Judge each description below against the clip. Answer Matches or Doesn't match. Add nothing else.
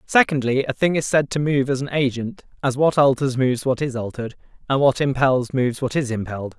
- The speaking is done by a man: Matches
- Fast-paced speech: Matches